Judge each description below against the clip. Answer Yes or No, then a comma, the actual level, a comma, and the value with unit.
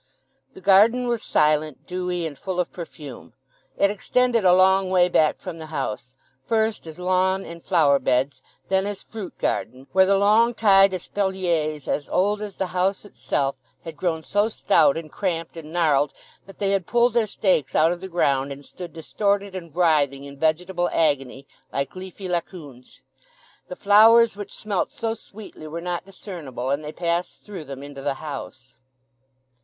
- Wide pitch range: No, average, 4.5 semitones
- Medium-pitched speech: Yes, medium, 180 Hz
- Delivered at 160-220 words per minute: Yes, average, 175 wpm